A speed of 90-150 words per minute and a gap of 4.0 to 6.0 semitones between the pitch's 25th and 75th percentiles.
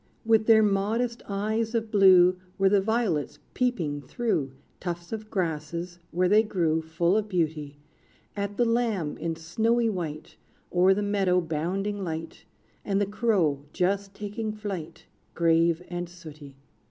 Yes: average, 140 wpm; average, 4.3 semitones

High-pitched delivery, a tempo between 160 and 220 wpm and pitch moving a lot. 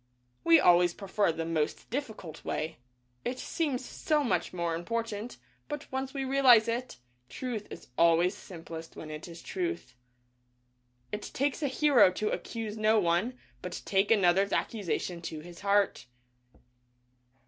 No: high, 205 Hz; average, 140 wpm; wide, 6.6 semitones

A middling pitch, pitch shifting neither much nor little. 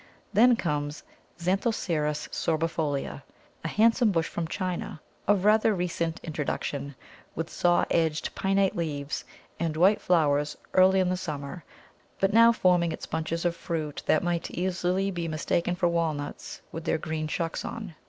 Yes: medium, 170 Hz; average, 3.1 semitones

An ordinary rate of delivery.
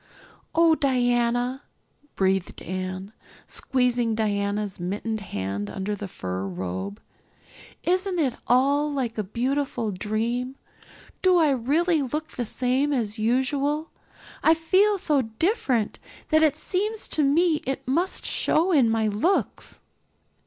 No: slow, 125 wpm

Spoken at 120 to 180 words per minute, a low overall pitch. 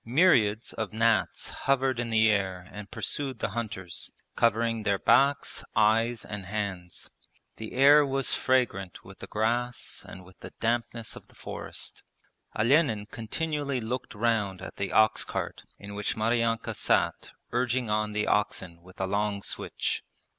Yes: average, 150 wpm; low, 110 Hz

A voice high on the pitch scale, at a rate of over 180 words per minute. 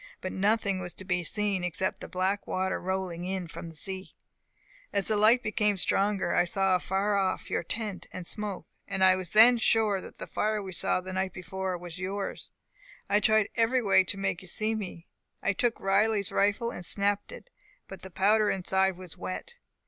Yes: high, 195 Hz; average, 195 wpm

